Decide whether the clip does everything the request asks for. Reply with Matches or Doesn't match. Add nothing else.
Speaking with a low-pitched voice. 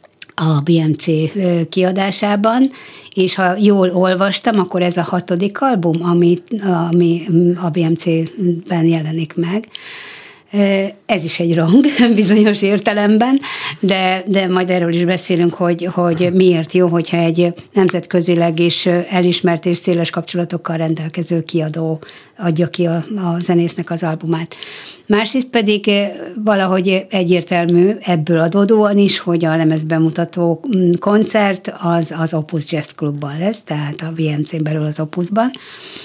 Doesn't match